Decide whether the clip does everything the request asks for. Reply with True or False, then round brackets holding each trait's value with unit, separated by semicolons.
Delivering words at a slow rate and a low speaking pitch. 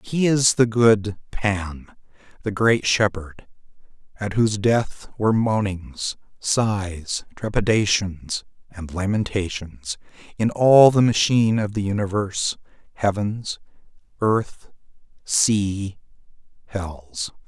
True (95 wpm; 100 Hz)